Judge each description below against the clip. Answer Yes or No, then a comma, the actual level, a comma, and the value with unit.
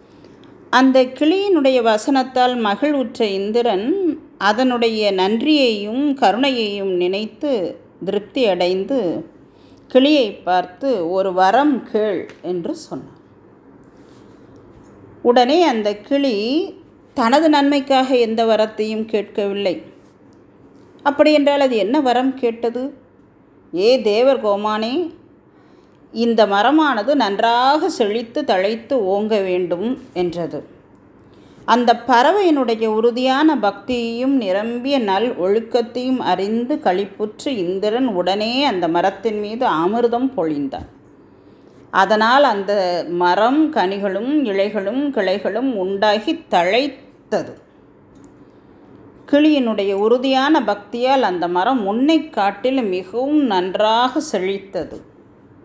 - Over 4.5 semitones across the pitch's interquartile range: Yes, average, 5.1 semitones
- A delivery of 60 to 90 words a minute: Yes, average, 85 wpm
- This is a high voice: Yes, high, 235 Hz